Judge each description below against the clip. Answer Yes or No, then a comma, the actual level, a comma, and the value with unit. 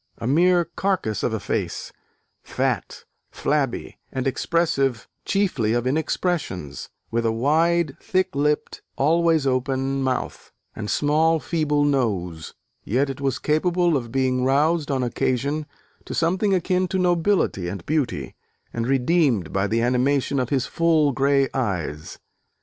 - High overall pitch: No, medium, 140 Hz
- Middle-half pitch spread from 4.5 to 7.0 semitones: Yes, average, 5.0 semitones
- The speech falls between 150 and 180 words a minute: No, slow, 135 wpm